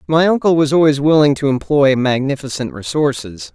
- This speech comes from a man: Yes, male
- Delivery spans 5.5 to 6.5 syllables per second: No, 5.3 syllables/s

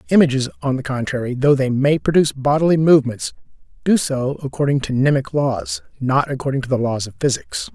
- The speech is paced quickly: No, average, 180 wpm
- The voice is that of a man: Yes, male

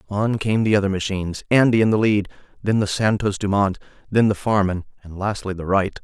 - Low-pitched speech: Yes, low, 100 Hz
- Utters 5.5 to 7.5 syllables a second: Yes, 5.7 syllables/s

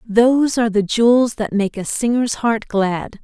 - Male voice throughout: No, female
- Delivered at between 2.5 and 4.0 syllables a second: No, 4.5 syllables/s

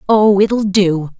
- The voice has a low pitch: No, high, 195 Hz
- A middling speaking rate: Yes, average, 150 wpm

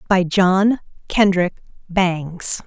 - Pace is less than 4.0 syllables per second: Yes, 2.5 syllables/s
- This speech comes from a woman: Yes, female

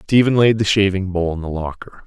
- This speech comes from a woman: No, male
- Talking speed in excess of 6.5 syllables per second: No, 5.6 syllables/s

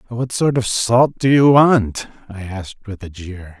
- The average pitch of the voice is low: Yes, low, 110 Hz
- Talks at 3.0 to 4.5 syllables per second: Yes, 4.2 syllables/s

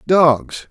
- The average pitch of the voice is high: No, medium, 150 Hz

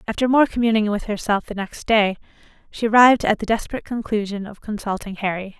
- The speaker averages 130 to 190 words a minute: Yes, average, 170 wpm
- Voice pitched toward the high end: Yes, high, 215 Hz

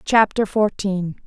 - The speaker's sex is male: No, female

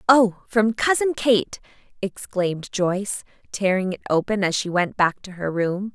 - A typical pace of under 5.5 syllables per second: Yes, 4.5 syllables/s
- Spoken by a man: No, female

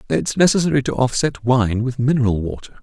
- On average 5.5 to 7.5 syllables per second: Yes, 5.8 syllables/s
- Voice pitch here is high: No, low, 125 Hz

